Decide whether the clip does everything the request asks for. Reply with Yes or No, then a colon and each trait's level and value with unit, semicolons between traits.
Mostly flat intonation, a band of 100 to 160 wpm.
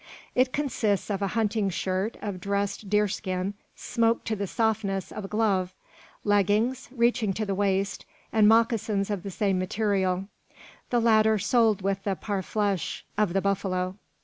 Yes: narrow, 2.3 semitones; average, 155 wpm